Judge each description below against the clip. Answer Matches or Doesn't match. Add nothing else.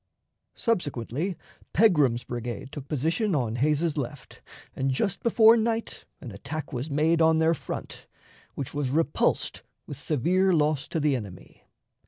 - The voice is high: Doesn't match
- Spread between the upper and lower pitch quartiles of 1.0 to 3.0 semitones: Doesn't match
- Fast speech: Doesn't match